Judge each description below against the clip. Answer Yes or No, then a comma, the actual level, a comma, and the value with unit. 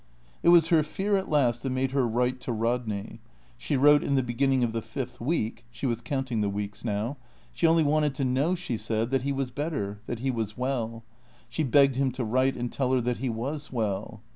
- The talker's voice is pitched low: Yes, low, 125 Hz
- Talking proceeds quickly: Yes, fast, 225 wpm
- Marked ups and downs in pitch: No, average, 3.3 semitones